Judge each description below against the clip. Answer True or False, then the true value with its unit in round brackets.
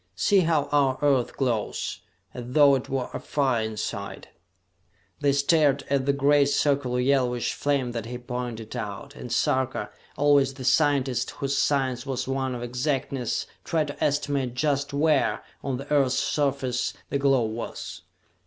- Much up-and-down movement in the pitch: False (2.4 semitones)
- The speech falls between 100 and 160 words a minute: True (150 wpm)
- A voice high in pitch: False (135 Hz)